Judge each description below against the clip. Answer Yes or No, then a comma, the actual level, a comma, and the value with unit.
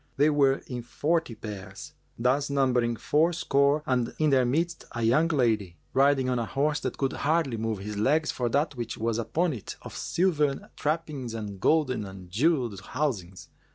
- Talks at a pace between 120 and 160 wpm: No, average, 170 wpm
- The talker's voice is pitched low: Yes, low, 130 Hz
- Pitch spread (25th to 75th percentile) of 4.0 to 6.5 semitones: Yes, average, 4.9 semitones